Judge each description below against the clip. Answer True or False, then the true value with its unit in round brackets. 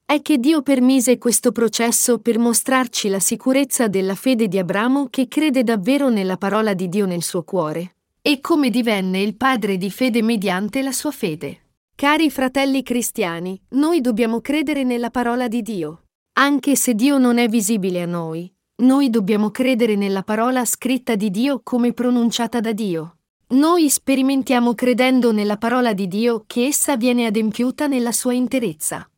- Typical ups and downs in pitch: True (3.7 semitones)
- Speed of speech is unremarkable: True (160 wpm)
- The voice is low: False (240 Hz)